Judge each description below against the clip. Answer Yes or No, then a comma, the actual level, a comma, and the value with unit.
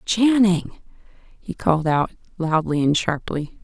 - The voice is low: No, medium, 175 Hz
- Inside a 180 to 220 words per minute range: No, slow, 115 wpm